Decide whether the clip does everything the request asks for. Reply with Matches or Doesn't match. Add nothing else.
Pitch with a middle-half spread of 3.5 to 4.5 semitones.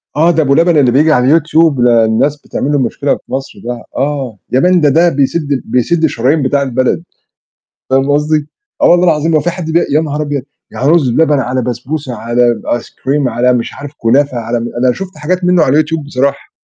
Matches